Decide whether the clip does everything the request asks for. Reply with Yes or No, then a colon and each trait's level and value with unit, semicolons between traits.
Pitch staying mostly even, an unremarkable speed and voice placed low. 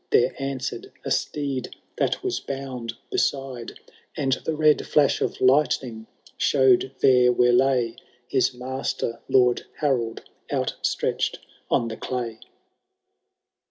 No: narrow, 1.9 semitones; slow, 115 wpm; low, 130 Hz